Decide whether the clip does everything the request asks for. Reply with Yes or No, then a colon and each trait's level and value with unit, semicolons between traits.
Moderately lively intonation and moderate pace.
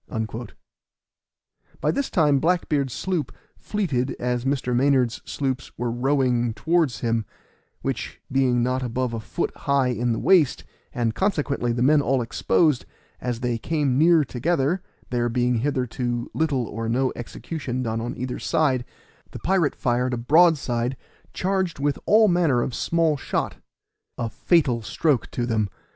Yes: average, 4.2 semitones; average, 150 wpm